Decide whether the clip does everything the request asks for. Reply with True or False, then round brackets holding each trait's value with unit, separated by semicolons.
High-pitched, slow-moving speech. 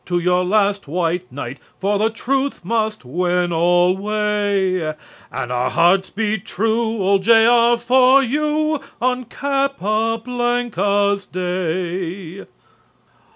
True (200 Hz; 110 wpm)